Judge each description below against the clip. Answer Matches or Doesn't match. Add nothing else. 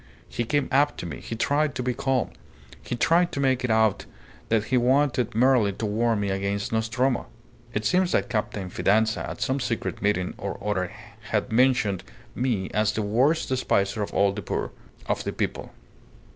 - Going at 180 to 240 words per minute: Matches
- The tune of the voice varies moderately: Matches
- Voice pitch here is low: Matches